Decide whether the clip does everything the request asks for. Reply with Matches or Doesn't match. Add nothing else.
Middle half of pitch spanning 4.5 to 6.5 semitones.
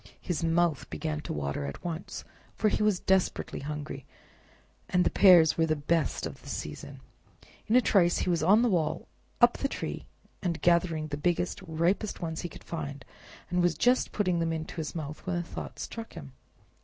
Doesn't match